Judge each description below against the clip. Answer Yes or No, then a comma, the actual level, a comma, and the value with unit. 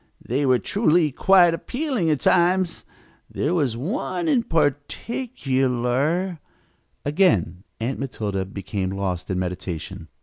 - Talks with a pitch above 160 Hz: No, medium, 145 Hz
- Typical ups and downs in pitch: No, wide, 8.5 semitones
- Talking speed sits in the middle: No, slow, 115 wpm